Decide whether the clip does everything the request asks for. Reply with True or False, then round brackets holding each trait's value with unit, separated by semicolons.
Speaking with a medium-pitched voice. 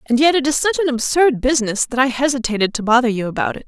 False (260 Hz)